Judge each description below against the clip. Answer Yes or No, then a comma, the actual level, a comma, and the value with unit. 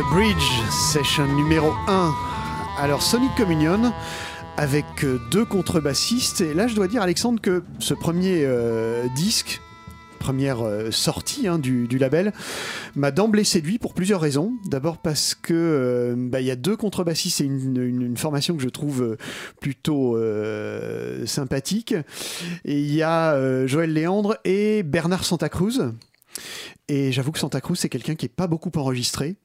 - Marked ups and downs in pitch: Yes, wide, 5.7 semitones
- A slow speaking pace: No, average, 155 wpm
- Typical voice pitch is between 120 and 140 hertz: No, medium, 150 Hz